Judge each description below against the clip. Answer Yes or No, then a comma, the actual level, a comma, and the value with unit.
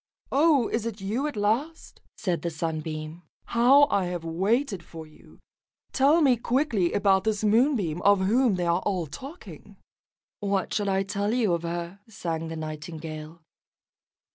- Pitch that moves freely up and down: Yes, wide, 5.7 semitones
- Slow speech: No, average, 155 wpm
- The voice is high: Yes, high, 195 Hz